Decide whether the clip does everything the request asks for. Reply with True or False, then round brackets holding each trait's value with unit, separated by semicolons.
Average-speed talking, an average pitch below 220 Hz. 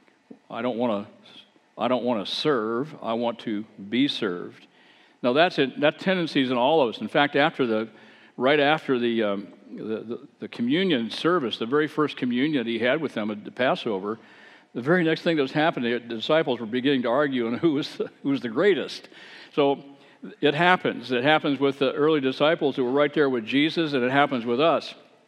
True (195 wpm; 140 Hz)